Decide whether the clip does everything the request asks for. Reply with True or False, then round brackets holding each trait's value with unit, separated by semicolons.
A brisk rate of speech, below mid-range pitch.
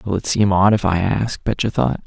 True (260 wpm; 100 Hz)